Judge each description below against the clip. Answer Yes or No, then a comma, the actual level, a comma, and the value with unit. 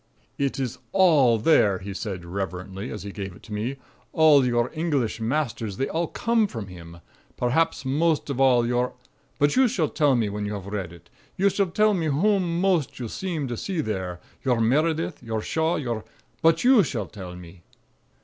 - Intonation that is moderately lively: No, wide, 7.7 semitones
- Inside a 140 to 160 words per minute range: No, average, 190 wpm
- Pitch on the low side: Yes, low, 125 Hz